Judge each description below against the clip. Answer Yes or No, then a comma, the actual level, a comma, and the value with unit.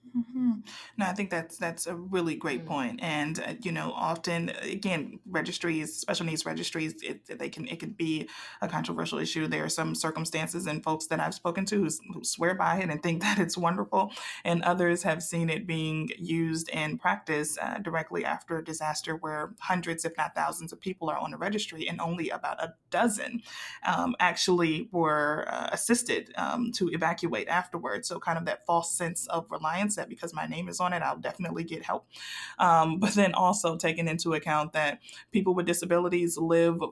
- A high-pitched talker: No, medium, 170 Hz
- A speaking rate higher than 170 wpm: Yes, average, 195 wpm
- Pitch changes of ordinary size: No, narrow, 2.3 semitones